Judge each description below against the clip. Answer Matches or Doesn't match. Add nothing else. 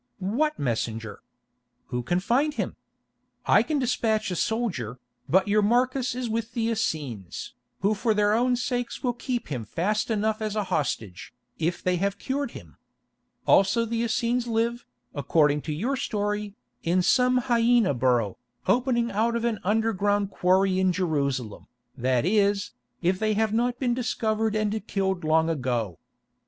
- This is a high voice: Matches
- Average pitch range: Doesn't match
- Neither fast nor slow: Matches